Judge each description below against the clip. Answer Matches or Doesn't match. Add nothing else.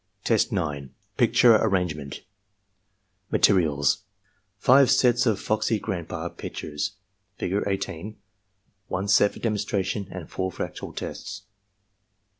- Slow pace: Matches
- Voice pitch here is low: Matches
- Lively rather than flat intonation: Doesn't match